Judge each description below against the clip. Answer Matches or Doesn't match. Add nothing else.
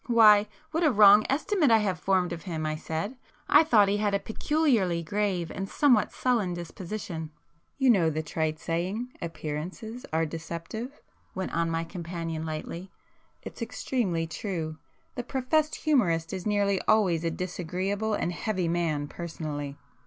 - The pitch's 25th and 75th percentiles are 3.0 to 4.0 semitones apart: Doesn't match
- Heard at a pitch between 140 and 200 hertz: Matches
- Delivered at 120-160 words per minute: Matches